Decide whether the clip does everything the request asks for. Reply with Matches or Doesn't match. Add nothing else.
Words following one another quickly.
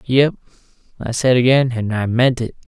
Doesn't match